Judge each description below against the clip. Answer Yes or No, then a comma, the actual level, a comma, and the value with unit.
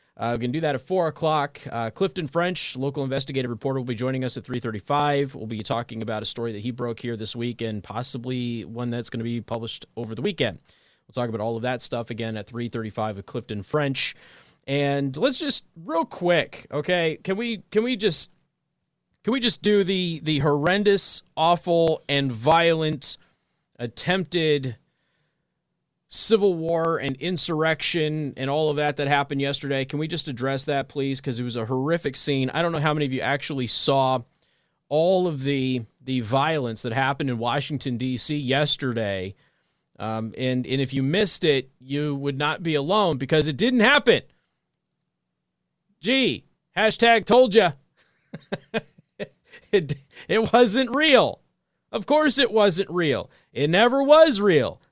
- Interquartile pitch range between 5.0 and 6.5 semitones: Yes, wide, 5.6 semitones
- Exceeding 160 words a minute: Yes, average, 170 wpm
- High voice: No, medium, 140 Hz